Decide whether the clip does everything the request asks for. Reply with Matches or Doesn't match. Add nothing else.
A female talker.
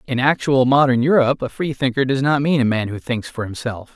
Doesn't match